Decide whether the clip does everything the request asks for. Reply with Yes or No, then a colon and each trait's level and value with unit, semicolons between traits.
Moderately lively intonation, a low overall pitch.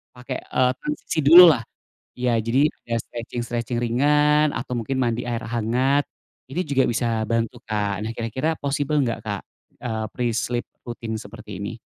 Yes: average, 3.2 semitones; low, 120 Hz